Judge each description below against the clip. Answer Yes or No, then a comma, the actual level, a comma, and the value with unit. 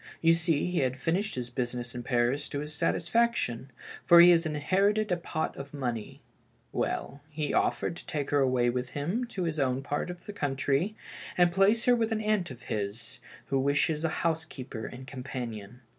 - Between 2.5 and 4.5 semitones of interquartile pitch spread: No, wide, 5.5 semitones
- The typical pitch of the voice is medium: Yes, medium, 145 Hz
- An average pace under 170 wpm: No, average, 190 wpm